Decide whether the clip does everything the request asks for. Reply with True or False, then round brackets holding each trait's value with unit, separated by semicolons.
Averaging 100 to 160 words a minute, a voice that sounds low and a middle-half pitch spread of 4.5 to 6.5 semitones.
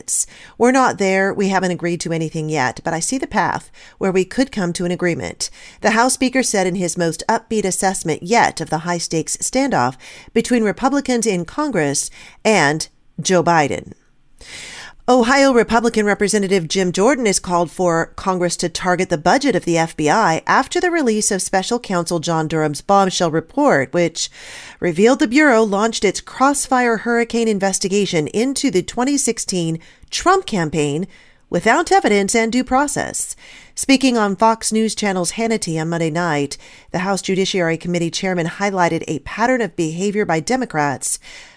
False (155 wpm; 195 Hz; 5.5 semitones)